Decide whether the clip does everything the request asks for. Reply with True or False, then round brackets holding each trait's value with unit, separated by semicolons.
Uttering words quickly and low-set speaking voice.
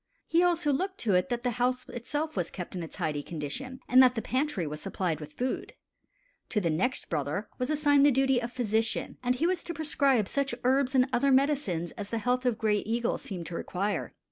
False (220 wpm; 245 Hz)